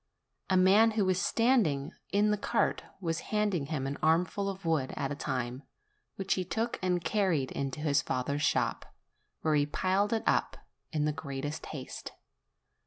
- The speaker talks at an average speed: Yes, average, 170 wpm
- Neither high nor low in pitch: Yes, medium, 165 Hz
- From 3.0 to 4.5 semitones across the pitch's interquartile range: No, wide, 5.4 semitones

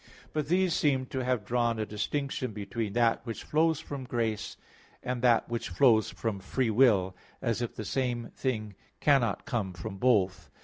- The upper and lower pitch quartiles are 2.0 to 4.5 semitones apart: Yes, average, 3.5 semitones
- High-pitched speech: No, low, 120 Hz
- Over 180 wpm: No, average, 170 wpm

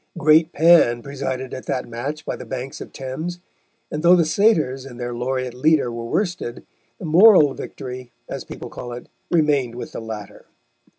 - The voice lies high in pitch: No, low, 135 Hz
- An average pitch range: Yes, average, 4.4 semitones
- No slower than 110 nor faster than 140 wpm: No, average, 175 wpm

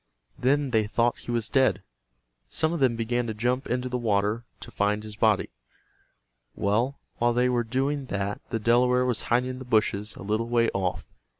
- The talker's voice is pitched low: Yes, low, 120 Hz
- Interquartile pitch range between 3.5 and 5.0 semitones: No, average, 2.9 semitones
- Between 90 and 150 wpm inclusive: No, average, 190 wpm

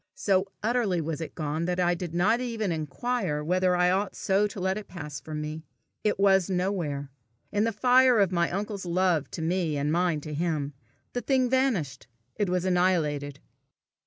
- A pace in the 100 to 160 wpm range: No, average, 185 wpm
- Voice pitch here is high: No, medium, 180 Hz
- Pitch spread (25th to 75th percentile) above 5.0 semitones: No, average, 4.3 semitones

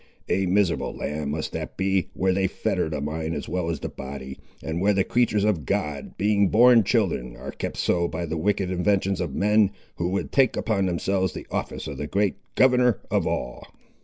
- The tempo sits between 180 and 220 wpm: Yes, average, 200 wpm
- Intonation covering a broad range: No, average, 4.3 semitones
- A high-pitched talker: No, very low, 95 Hz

